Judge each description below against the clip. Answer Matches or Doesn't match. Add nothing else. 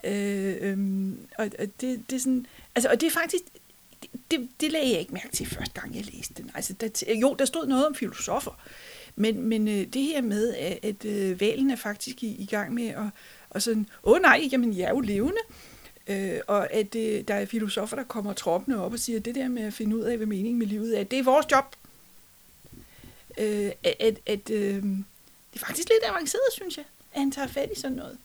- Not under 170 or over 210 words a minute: Doesn't match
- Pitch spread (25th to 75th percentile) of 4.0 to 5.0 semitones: Matches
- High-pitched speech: Matches